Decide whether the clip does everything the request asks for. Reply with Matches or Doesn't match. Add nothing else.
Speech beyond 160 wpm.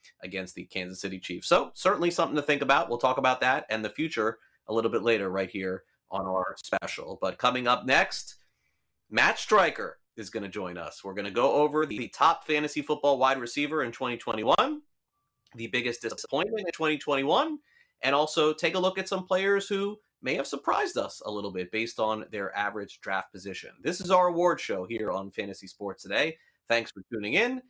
Matches